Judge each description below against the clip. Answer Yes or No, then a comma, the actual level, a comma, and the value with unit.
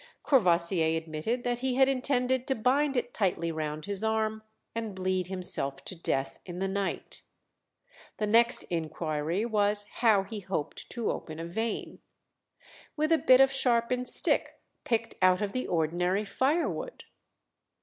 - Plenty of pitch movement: Yes, wide, 6.1 semitones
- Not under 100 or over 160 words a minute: Yes, average, 150 wpm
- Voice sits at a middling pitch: No, high, 210 Hz